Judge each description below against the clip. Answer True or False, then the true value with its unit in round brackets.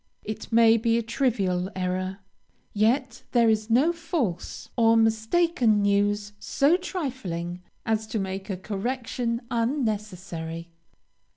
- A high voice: True (220 Hz)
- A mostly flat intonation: False (3.8 semitones)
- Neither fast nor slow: False (115 wpm)